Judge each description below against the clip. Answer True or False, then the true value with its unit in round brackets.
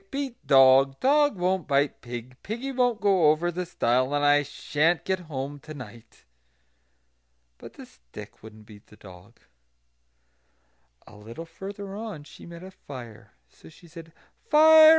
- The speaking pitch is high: False (155 Hz)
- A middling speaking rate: True (150 wpm)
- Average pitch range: False (7.4 semitones)